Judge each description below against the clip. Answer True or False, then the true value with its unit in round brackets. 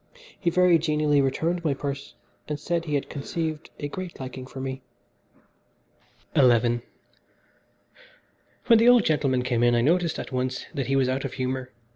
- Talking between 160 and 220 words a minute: True (165 wpm)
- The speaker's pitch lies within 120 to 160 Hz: True (140 Hz)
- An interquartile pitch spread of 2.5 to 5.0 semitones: True (4.3 semitones)